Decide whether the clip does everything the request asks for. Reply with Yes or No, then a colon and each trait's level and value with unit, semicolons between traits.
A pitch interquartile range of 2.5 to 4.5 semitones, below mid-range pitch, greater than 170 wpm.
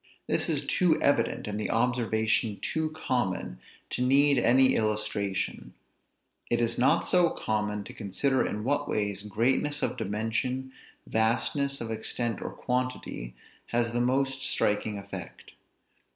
No: average, 3.8 semitones; low, 120 Hz; slow, 135 wpm